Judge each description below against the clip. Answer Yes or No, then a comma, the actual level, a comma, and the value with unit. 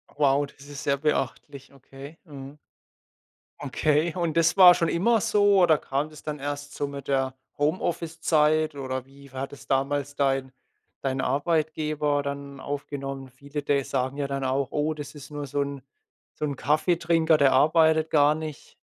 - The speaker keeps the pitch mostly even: Yes, narrow, 2.1 semitones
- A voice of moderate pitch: Yes, medium, 145 Hz